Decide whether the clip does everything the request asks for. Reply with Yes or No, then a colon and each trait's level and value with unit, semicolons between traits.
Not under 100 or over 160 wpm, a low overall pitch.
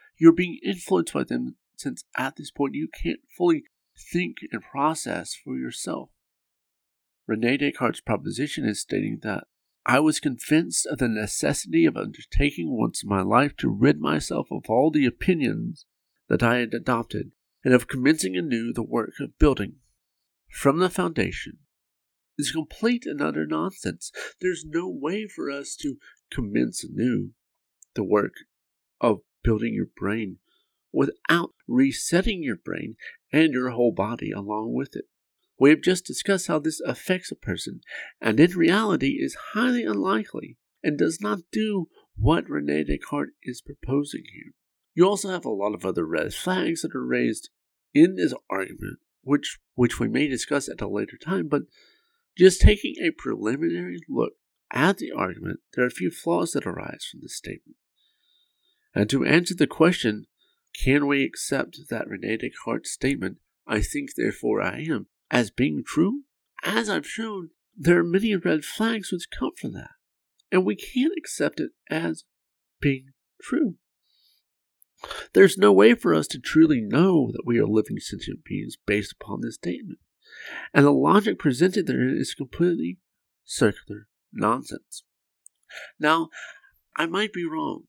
No: average, 155 wpm; medium, 165 Hz